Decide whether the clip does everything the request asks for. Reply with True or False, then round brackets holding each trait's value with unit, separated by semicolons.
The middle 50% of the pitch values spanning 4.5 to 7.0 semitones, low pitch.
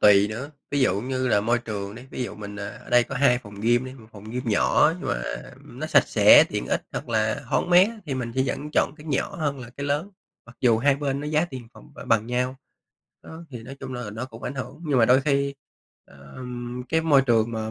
False (3.8 semitones; 125 Hz)